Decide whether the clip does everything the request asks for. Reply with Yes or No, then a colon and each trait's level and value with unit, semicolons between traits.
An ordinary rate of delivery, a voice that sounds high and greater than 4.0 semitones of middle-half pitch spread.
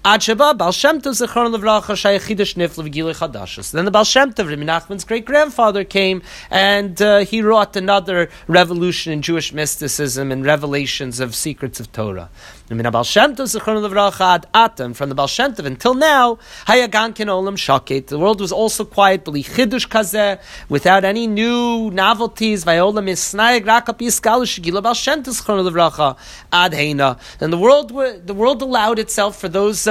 No: slow, 90 wpm; high, 200 Hz; wide, 5.5 semitones